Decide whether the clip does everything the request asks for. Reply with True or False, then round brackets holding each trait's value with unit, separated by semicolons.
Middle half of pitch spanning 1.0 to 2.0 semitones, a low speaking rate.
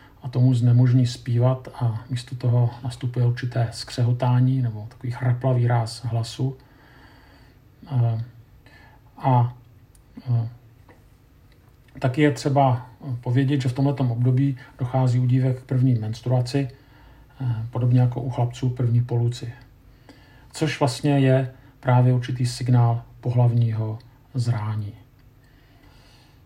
True (1.5 semitones; 100 wpm)